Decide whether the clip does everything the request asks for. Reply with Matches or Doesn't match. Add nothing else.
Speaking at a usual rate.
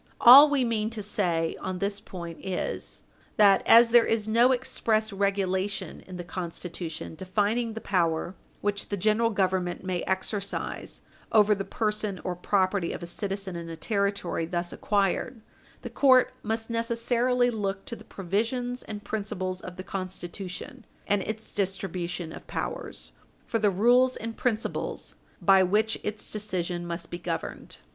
Matches